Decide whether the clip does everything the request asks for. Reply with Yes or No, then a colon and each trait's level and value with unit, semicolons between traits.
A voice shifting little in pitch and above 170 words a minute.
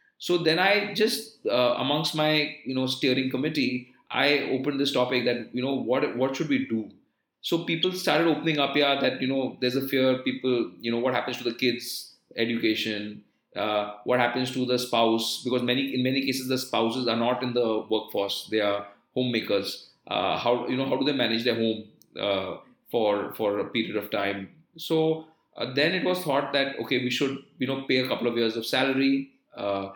No: average, 3.3 semitones; fast, 205 wpm